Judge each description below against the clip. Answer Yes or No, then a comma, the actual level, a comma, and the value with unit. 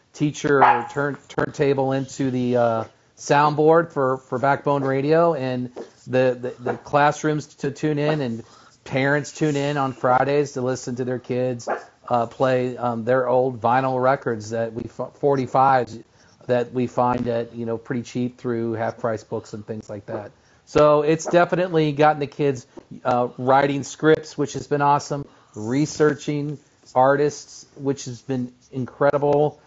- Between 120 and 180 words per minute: Yes, average, 150 wpm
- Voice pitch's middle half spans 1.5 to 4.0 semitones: Yes, average, 2.9 semitones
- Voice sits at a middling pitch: No, low, 130 Hz